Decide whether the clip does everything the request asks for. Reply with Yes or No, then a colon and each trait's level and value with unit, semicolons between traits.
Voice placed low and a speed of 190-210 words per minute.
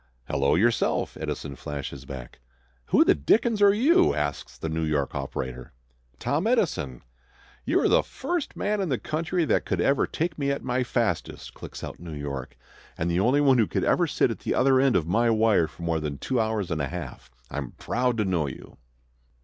Yes: low, 105 Hz; average, 200 wpm